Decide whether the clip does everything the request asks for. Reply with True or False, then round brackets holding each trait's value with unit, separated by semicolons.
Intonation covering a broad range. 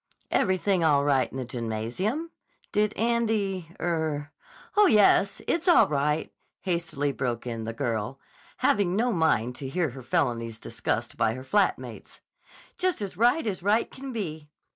True (8.4 semitones)